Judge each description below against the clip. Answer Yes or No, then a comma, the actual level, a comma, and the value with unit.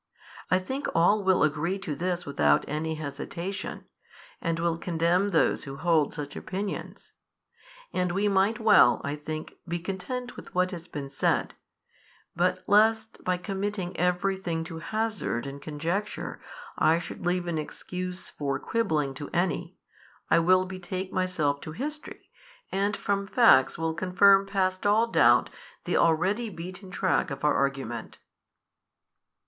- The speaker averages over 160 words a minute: No, average, 145 wpm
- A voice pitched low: No, medium, 180 Hz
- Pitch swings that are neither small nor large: Yes, average, 3.6 semitones